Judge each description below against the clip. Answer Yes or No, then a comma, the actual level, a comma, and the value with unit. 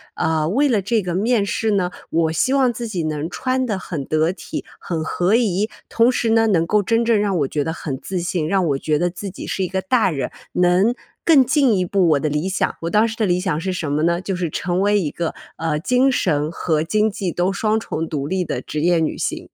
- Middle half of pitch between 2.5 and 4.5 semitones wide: No, average, 5.0 semitones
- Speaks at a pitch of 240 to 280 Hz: No, medium, 185 Hz